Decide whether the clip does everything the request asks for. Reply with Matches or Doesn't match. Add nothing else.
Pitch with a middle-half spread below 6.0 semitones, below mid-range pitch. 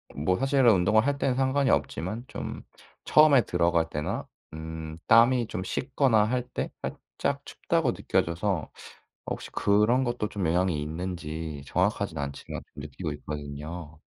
Doesn't match